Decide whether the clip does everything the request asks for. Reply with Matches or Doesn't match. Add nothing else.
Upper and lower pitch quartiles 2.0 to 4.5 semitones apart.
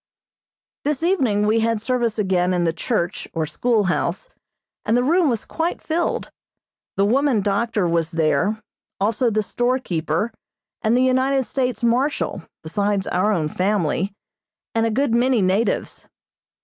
Doesn't match